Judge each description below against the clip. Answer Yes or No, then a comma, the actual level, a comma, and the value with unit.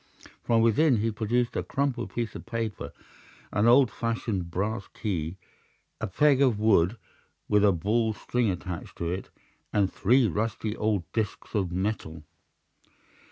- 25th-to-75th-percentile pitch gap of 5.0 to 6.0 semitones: No, average, 3.5 semitones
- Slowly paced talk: No, average, 150 wpm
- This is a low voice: Yes, low, 110 Hz